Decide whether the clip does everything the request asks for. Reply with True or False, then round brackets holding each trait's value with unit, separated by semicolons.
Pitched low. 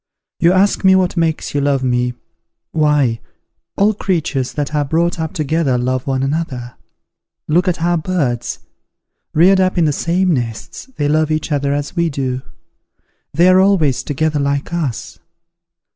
False (155 Hz)